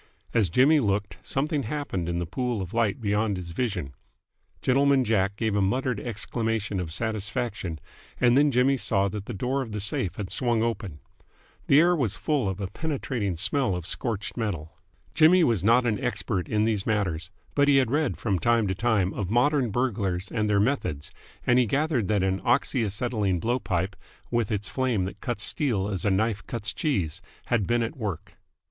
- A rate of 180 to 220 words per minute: Yes, average, 190 wpm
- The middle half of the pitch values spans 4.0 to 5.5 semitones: Yes, average, 4.5 semitones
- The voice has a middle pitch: No, low, 110 Hz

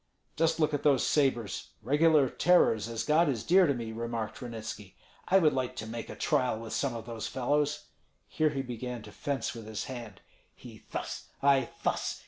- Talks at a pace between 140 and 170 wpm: No, average, 190 wpm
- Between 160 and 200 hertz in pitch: No, low, 125 Hz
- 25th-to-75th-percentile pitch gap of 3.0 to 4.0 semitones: No, average, 4.4 semitones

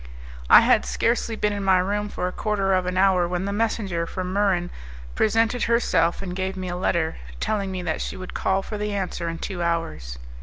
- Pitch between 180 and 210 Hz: Yes, high, 190 Hz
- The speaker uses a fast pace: Yes, fast, 215 wpm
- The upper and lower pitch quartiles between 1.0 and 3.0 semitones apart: Yes, narrow, 2.5 semitones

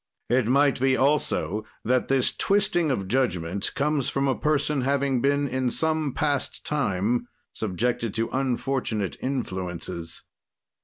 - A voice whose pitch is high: No, low, 130 Hz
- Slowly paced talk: Yes, slow, 125 wpm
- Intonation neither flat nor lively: Yes, average, 4.1 semitones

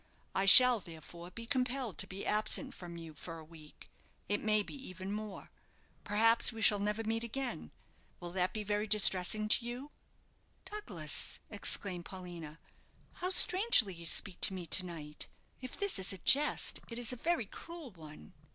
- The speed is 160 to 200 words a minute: Yes, average, 170 wpm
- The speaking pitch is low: No, high, 205 Hz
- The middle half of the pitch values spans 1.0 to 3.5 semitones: No, average, 4.9 semitones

